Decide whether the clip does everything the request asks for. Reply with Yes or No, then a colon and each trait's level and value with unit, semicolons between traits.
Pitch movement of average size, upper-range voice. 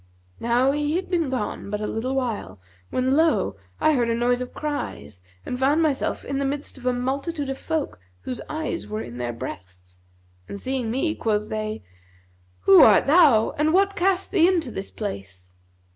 No: wide, 6.3 semitones; very high, 255 Hz